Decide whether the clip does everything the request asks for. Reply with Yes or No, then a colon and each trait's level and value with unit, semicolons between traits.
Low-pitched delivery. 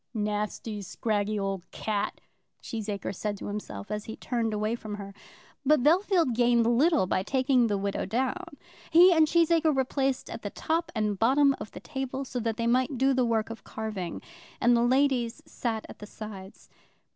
No: high, 235 Hz